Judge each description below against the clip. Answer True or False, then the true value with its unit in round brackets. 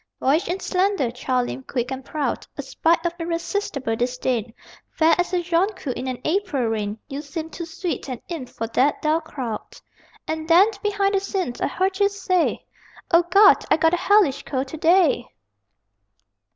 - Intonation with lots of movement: True (5.9 semitones)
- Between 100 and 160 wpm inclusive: False (180 wpm)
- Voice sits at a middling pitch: False (320 Hz)